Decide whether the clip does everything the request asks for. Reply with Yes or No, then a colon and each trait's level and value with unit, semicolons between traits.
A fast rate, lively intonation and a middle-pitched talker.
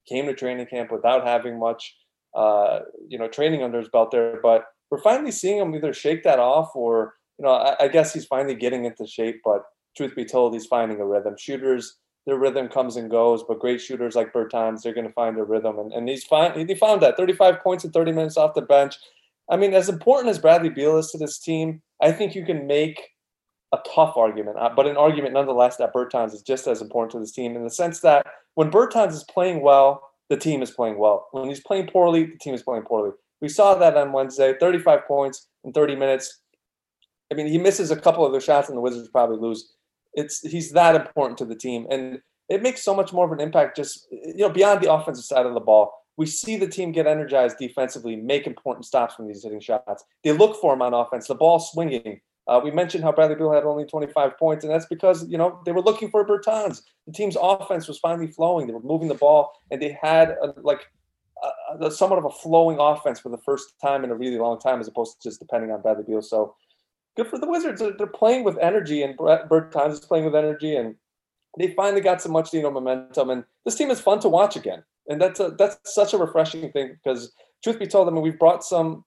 Yes: fast, 235 wpm; wide, 5.7 semitones; medium, 150 Hz